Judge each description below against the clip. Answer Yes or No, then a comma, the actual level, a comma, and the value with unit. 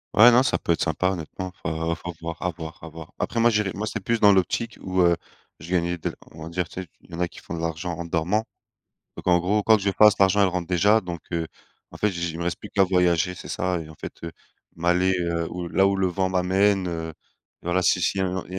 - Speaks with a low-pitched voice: Yes, very low, 90 Hz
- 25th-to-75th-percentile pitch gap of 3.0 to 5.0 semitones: No, narrow, 2.4 semitones